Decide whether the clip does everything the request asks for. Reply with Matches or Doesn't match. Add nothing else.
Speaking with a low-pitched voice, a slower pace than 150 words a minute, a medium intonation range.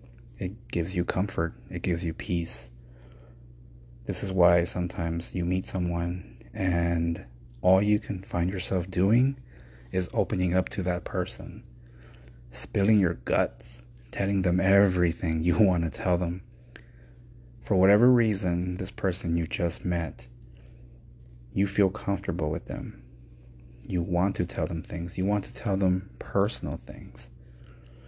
Doesn't match